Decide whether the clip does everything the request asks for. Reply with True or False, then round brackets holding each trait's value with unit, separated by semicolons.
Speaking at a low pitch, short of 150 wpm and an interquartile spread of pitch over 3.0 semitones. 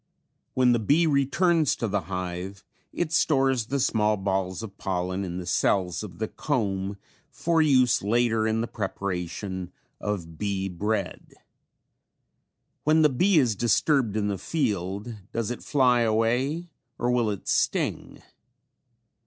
True (110 Hz; 140 wpm; 5.2 semitones)